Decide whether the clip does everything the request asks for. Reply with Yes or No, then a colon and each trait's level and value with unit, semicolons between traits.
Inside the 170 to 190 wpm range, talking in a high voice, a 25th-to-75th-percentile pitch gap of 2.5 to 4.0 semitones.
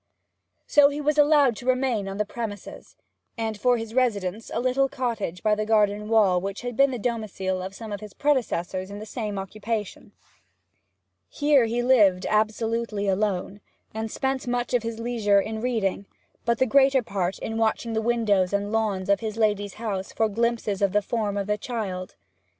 Yes: average, 185 wpm; high, 220 Hz; average, 3.0 semitones